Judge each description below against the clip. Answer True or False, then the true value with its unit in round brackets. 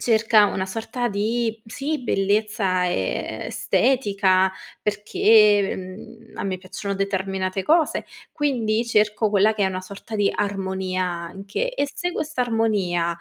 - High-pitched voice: True (205 Hz)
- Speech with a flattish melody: False (3.0 semitones)